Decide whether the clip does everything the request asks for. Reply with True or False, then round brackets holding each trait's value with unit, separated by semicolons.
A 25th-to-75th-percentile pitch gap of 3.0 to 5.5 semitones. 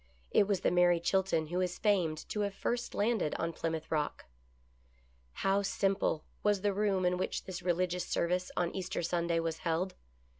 False (2.5 semitones)